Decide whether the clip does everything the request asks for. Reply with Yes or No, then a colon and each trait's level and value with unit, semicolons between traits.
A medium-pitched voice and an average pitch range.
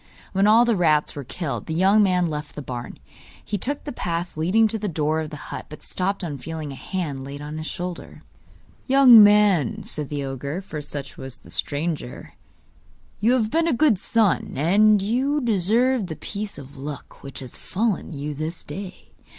No: medium, 175 Hz; wide, 6.2 semitones